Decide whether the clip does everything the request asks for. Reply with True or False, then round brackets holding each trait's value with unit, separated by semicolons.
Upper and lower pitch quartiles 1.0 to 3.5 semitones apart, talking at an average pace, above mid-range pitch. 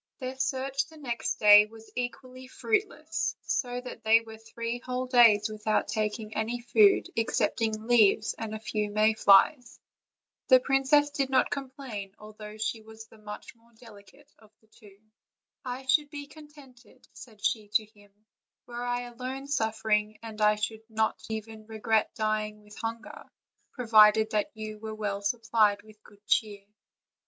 True (2.8 semitones; 155 wpm; 220 Hz)